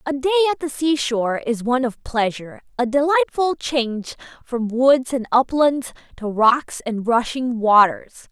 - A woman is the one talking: Yes, female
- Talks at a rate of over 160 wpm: No, average, 150 wpm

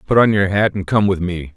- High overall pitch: No, very low, 95 Hz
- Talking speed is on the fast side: Yes, fast, 310 wpm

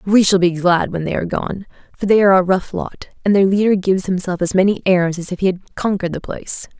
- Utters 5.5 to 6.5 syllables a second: Yes, 6.2 syllables/s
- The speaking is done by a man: No, female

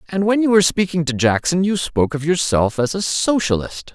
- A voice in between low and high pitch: Yes, medium, 165 Hz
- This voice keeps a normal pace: No, fast, 215 wpm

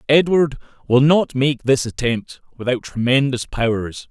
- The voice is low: Yes, low, 130 Hz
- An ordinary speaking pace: No, slow, 130 wpm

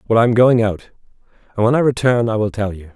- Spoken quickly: Yes, fast, 265 wpm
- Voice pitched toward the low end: Yes, low, 110 Hz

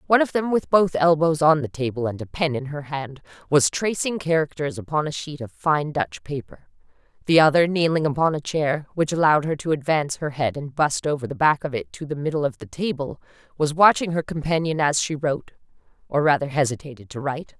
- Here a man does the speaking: No, female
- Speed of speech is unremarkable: No, fast, 215 wpm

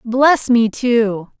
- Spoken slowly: Yes, slow, 130 wpm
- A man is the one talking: No, female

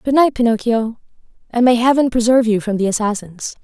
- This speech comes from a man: No, female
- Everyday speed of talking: Yes, average, 180 wpm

